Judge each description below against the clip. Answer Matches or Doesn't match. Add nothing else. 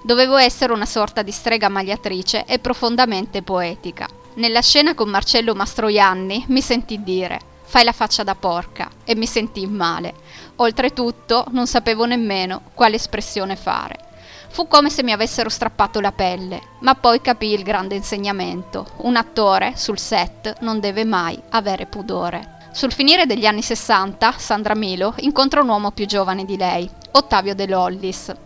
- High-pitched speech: Matches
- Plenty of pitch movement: Doesn't match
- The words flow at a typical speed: Matches